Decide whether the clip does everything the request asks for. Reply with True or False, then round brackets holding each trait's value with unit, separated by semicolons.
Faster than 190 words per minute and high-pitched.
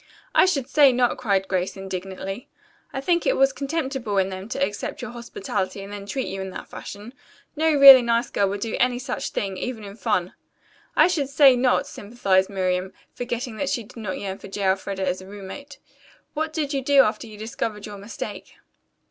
True (200 wpm; 220 Hz)